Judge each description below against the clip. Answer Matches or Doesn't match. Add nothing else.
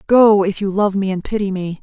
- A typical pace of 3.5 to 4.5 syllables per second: Doesn't match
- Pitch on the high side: Matches